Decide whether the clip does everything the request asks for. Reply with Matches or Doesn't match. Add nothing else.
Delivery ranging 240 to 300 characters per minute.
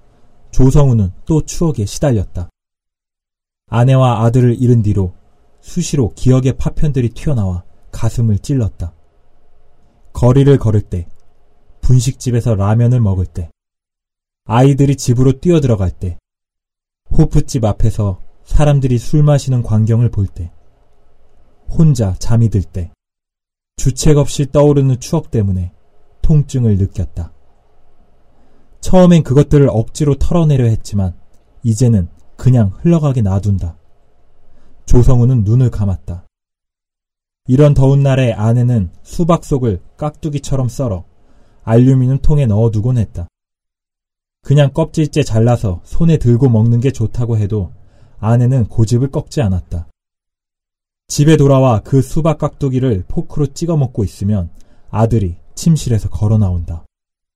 Matches